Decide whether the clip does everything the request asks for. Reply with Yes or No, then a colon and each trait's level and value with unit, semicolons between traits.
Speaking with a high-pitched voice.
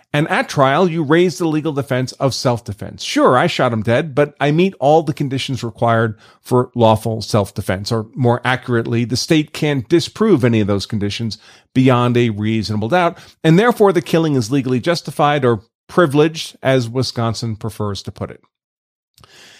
No: low, 125 Hz